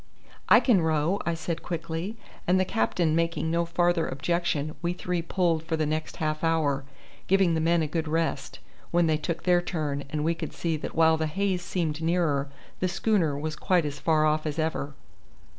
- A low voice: No, medium, 165 Hz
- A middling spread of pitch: No, narrow, 2.1 semitones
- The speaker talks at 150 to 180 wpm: No, average, 195 wpm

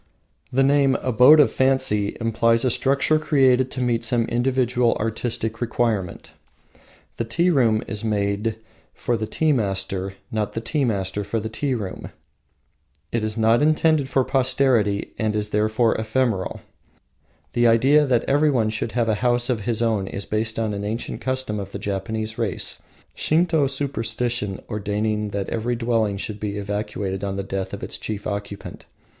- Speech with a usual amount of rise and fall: Yes, average, 3.6 semitones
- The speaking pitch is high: No, low, 115 Hz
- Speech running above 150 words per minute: Yes, average, 160 wpm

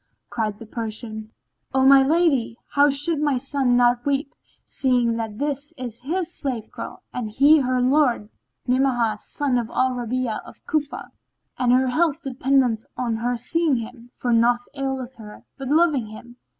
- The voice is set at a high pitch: Yes, very high, 255 Hz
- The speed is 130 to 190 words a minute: Yes, average, 165 wpm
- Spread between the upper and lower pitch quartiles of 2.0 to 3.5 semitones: Yes, average, 3.1 semitones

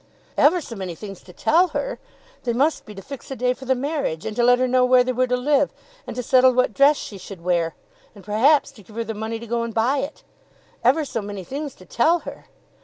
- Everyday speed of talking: No, fast, 255 wpm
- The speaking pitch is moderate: No, very high, 250 Hz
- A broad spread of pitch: No, average, 4.5 semitones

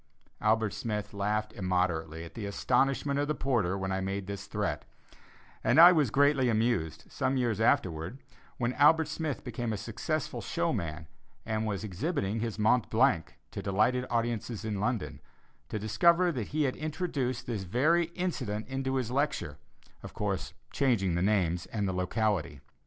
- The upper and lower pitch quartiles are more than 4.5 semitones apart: Yes, wide, 5.4 semitones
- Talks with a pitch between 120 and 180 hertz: No, low, 110 Hz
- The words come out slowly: No, average, 155 wpm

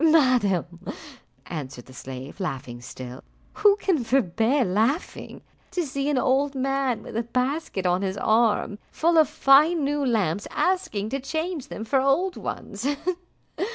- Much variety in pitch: Yes, wide, 7.1 semitones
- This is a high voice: Yes, very high, 255 Hz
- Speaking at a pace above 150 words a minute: No, average, 145 wpm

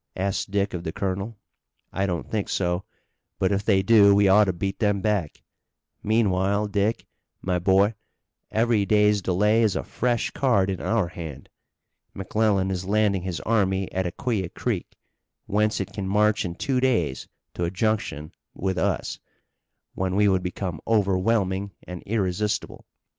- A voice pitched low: Yes, low, 100 Hz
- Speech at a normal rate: Yes, average, 155 wpm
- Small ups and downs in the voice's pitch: Yes, narrow, 2.3 semitones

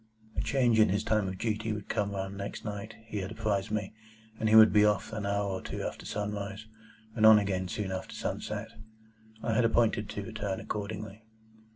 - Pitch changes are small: Yes, narrow, 1.7 semitones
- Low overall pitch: Yes, low, 105 Hz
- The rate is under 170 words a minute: No, average, 200 wpm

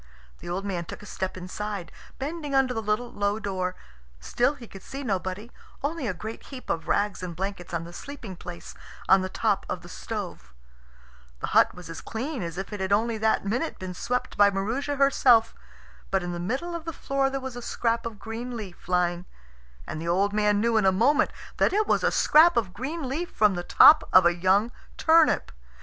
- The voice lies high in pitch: Yes, high, 210 Hz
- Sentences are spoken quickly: Yes, fast, 210 wpm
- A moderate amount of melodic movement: No, wide, 5.8 semitones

